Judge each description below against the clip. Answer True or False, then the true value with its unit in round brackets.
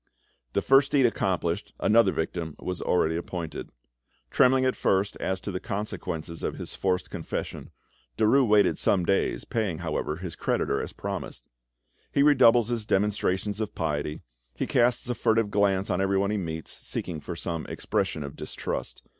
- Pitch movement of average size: True (4.5 semitones)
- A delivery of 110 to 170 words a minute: True (160 wpm)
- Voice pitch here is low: True (95 Hz)